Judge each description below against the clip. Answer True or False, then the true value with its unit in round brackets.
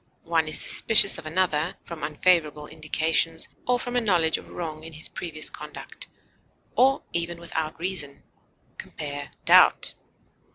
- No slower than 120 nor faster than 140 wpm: True (135 wpm)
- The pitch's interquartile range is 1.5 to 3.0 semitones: True (2.6 semitones)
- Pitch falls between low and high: True (165 Hz)